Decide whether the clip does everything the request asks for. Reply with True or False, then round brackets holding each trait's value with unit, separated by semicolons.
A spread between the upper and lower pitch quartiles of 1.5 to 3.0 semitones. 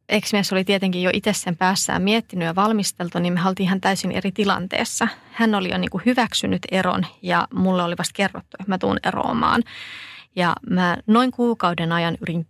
True (2.5 semitones)